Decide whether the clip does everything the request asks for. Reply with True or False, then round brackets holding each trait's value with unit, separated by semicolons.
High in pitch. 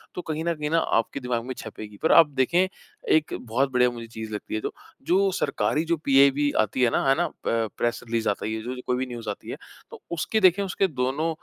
False (130 Hz)